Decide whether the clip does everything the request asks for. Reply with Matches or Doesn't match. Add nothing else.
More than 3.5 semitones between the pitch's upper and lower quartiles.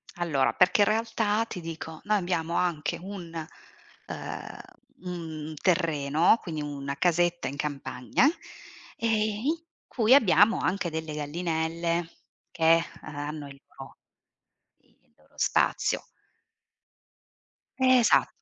Matches